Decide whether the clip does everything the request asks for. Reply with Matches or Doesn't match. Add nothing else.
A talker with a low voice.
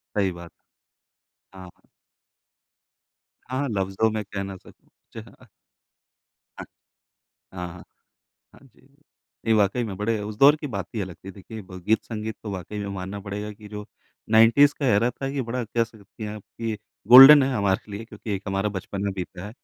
Matches